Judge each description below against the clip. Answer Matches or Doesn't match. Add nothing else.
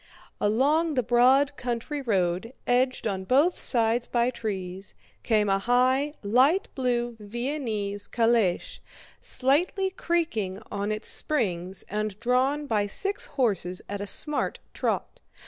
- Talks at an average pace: Doesn't match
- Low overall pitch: Doesn't match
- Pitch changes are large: Doesn't match